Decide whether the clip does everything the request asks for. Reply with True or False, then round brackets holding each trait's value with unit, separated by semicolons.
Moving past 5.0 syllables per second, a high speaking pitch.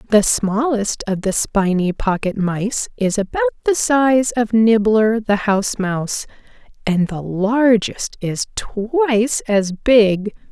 False (3.6 syllables/s; 220 Hz)